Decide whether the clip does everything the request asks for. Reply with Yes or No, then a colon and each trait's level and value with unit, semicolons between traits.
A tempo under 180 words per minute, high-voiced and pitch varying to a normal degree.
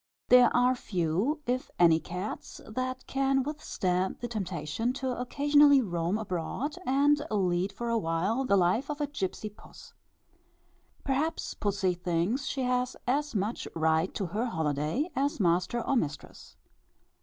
No: average, 145 wpm; high, 225 Hz; wide, 6.8 semitones